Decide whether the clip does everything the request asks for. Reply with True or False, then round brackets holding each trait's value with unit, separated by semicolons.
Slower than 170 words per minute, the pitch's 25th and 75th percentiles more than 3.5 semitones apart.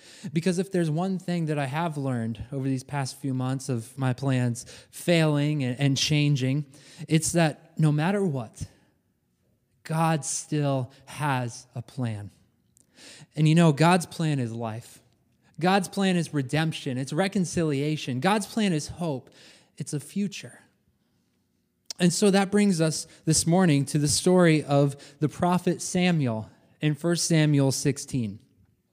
True (140 wpm; 4.4 semitones)